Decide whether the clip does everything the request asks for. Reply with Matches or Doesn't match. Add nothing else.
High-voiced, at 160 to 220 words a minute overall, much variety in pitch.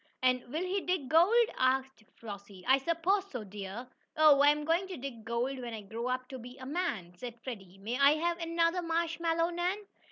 Matches